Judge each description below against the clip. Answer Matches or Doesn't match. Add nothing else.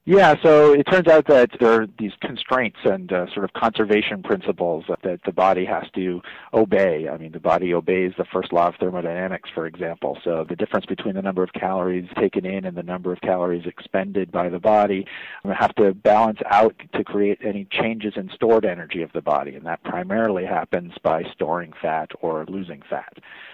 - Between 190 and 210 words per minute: Matches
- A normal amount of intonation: Matches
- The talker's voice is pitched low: Matches